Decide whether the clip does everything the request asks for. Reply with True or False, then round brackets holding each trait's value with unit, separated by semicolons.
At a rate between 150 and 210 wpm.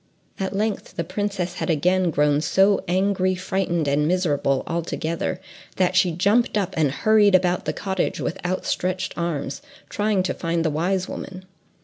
True (160 wpm)